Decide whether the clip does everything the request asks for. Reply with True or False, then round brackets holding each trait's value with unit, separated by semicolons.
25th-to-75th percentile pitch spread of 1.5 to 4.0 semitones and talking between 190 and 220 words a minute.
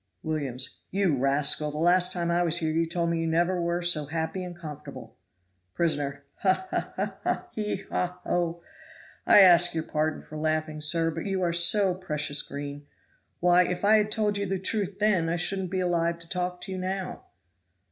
True (2.9 semitones; 200 wpm)